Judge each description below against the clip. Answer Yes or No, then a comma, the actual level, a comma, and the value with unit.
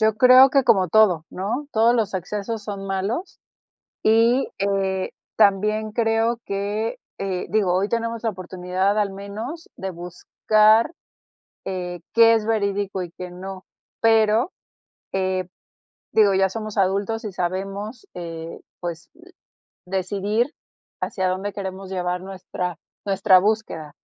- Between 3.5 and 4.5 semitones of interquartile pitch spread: No, average, 2.9 semitones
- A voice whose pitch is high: Yes, high, 200 Hz